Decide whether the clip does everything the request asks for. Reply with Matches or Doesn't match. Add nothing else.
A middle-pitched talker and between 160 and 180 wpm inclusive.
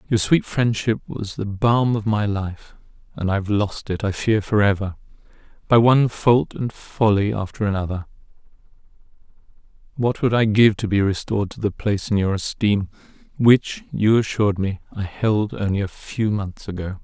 Doesn't match